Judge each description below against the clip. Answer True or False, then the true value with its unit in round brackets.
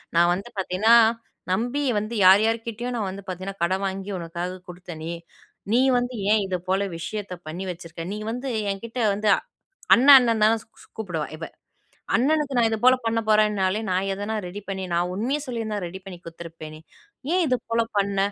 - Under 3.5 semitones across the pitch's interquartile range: False (3.9 semitones)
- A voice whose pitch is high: True (200 Hz)